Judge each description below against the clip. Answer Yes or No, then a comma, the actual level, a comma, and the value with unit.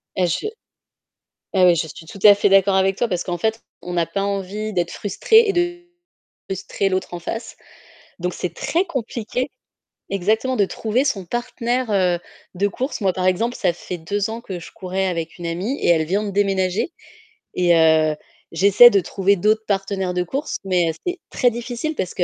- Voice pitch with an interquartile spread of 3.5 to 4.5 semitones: Yes, average, 4.1 semitones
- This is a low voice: No, high, 195 Hz